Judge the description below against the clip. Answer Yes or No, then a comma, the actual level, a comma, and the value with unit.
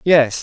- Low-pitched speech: No, medium, 145 Hz